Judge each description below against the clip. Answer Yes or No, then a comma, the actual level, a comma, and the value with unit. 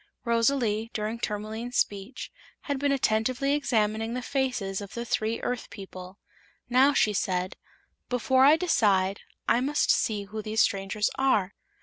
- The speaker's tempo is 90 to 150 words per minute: Yes, average, 140 wpm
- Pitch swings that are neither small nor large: Yes, average, 3.8 semitones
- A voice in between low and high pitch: No, high, 225 Hz